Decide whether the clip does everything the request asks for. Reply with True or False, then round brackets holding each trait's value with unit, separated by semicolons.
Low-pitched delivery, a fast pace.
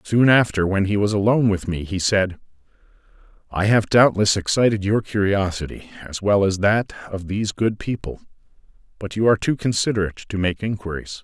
False (100 Hz; 170 wpm)